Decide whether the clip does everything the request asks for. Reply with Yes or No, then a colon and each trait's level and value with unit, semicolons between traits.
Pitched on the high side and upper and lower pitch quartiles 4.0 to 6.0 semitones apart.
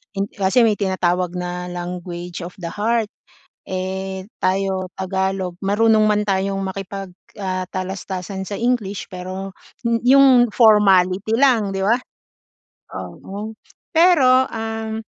No: high, 195 Hz; average, 3.0 semitones